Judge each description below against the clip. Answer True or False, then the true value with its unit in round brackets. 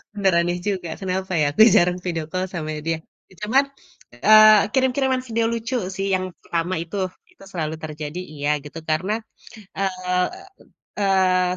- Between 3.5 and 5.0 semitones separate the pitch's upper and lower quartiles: True (3.9 semitones)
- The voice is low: False (185 Hz)